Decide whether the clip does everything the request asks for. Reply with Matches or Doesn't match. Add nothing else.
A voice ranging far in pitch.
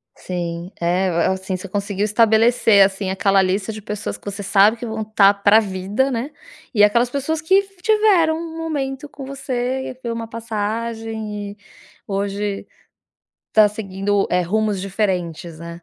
Doesn't match